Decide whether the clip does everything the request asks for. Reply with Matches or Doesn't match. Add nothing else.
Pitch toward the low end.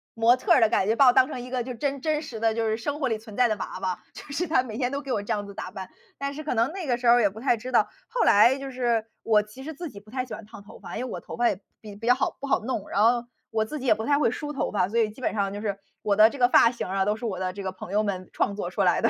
Doesn't match